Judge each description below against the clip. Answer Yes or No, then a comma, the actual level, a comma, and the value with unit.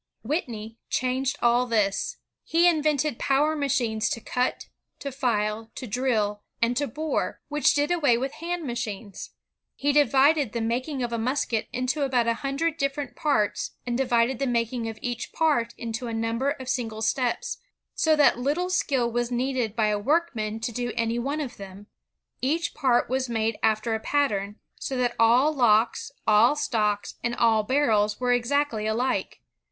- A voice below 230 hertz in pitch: No, high, 245 Hz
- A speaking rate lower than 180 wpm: Yes, average, 170 wpm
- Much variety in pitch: No, average, 3.8 semitones